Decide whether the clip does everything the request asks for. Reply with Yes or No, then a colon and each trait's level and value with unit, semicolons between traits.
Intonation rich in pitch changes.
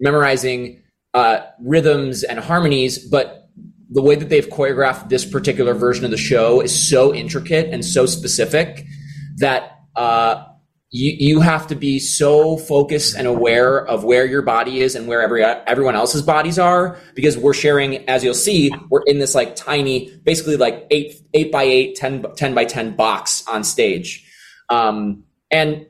No: average, 3.2 semitones